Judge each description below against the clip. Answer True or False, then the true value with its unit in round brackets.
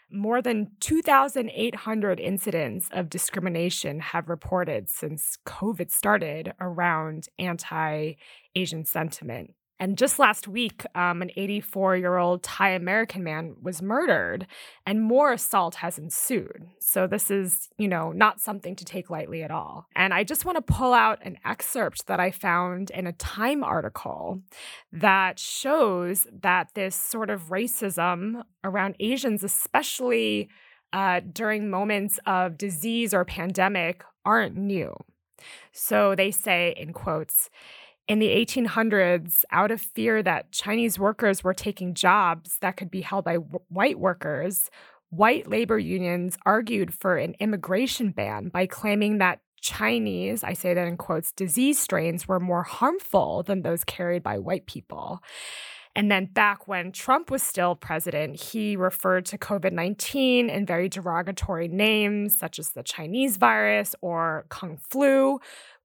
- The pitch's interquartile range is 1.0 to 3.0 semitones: False (3.5 semitones)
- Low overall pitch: False (190 Hz)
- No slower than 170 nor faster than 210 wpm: False (140 wpm)